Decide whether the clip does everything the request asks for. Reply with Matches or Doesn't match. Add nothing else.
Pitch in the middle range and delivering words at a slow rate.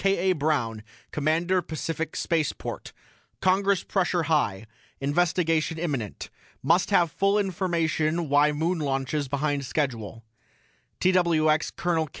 Matches